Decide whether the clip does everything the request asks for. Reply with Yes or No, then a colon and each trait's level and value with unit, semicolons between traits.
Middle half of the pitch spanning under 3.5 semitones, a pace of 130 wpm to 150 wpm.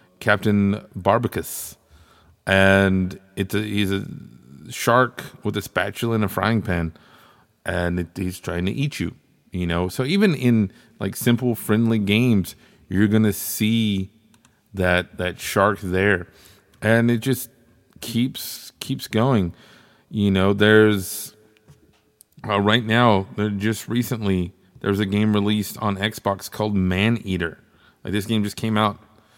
Yes: narrow, 2.6 semitones; average, 140 wpm